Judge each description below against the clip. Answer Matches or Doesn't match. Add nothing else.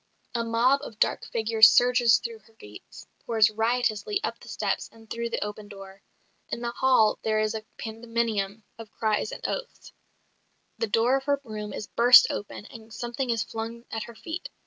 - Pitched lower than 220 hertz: Doesn't match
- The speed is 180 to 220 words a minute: Matches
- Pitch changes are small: Matches